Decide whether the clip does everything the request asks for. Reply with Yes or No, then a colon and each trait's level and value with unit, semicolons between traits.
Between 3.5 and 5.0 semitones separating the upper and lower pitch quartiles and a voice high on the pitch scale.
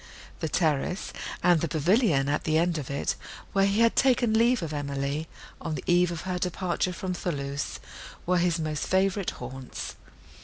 No: average, 4.1 semitones; medium, 170 Hz